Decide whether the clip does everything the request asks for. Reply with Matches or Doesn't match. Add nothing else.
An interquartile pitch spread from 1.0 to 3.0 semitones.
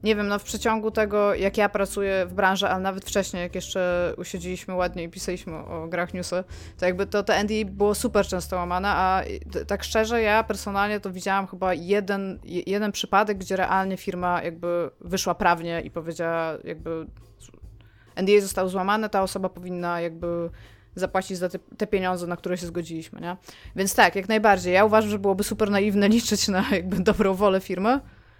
Matches